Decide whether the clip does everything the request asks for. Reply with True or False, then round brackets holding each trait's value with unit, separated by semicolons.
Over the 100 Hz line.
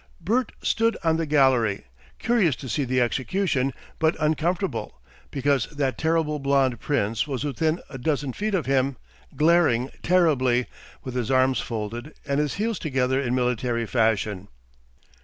True (140 Hz)